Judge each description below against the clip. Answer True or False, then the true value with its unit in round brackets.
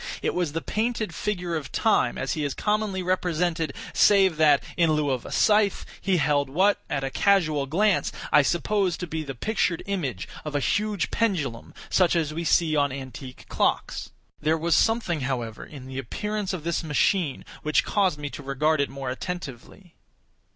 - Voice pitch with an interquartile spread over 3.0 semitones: True (5.0 semitones)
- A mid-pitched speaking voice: True (160 Hz)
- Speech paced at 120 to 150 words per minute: False (180 wpm)